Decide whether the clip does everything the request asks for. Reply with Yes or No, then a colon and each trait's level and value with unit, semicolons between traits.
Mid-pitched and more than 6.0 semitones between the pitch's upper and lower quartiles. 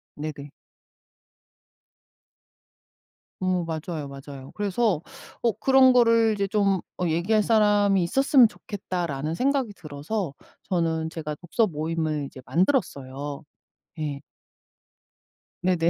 No: medium, 175 Hz; wide, 5.7 semitones